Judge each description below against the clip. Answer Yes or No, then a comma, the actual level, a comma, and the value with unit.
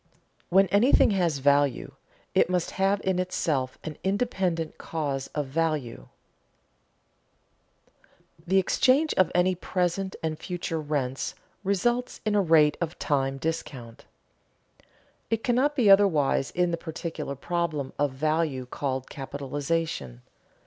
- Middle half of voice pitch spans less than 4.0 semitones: No, average, 5.0 semitones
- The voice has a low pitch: No, medium, 165 Hz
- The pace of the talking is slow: Yes, slow, 125 wpm